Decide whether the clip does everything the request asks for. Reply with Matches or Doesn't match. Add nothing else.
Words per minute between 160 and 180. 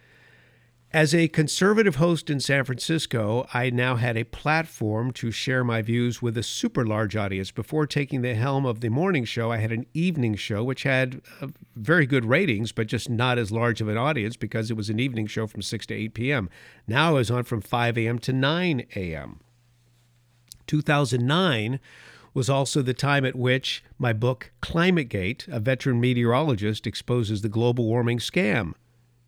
Matches